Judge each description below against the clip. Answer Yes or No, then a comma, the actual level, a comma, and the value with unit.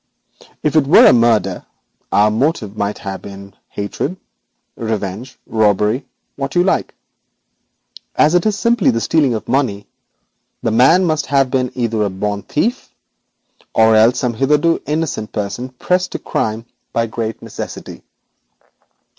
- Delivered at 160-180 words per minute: No, average, 140 wpm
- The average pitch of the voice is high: No, low, 120 Hz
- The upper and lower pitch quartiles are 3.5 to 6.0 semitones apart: Yes, wide, 5.6 semitones